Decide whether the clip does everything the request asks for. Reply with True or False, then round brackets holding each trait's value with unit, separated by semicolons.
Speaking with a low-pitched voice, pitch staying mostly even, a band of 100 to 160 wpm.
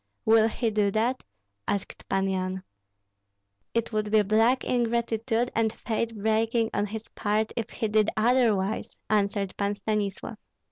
False (220 Hz; 1.8 semitones; 140 wpm)